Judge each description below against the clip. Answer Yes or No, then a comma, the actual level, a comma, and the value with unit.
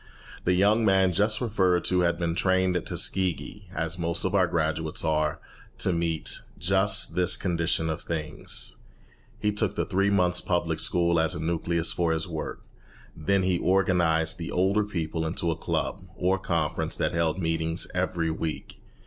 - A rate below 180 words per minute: Yes, average, 165 wpm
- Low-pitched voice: Yes, very low, 85 Hz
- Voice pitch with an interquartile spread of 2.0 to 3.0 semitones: Yes, narrow, 2.6 semitones